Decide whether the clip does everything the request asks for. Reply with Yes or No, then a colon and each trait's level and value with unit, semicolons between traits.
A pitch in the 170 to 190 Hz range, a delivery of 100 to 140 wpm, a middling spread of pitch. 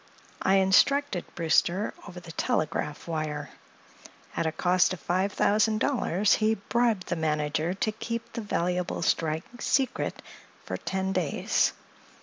Yes: medium, 185 Hz; slow, 135 wpm; average, 4.7 semitones